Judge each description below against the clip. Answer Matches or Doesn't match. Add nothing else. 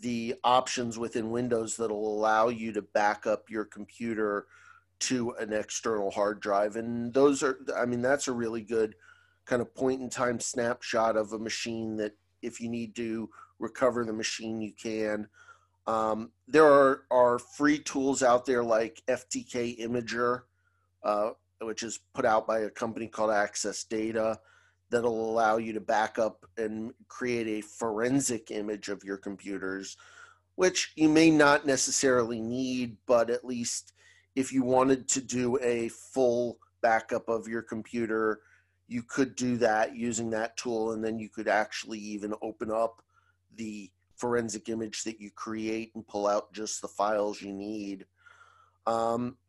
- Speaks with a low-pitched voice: Matches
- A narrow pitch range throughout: Matches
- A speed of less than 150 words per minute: Doesn't match